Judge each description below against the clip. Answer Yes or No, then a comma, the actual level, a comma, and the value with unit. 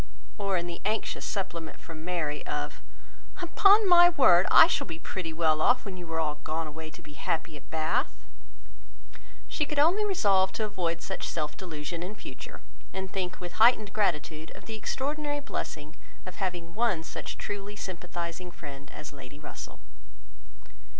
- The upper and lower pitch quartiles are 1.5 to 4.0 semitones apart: No, average, 4.9 semitones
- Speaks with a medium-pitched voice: Yes, medium, 175 Hz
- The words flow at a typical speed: Yes, average, 165 wpm